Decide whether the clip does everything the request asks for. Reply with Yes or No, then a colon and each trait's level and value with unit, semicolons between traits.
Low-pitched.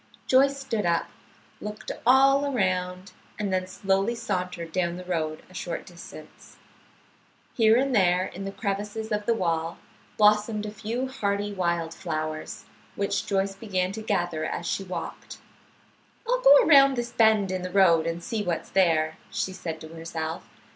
No: high, 195 Hz